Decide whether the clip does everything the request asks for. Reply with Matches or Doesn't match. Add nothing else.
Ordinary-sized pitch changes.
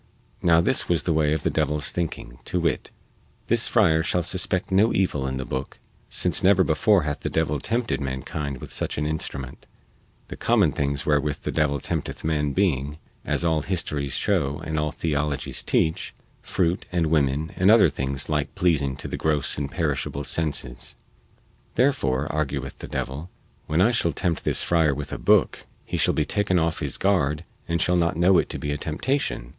Matches